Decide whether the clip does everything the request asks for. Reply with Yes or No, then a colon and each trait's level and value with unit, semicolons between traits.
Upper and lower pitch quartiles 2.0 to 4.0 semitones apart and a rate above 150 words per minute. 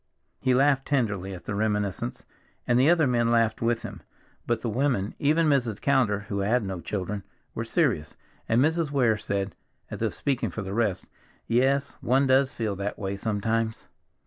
No: average, 4.6 semitones; average, 175 wpm